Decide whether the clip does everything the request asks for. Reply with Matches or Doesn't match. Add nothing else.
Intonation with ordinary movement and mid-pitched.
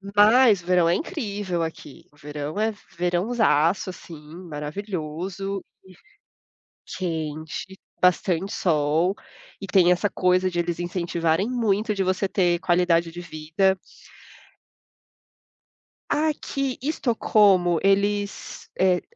Matches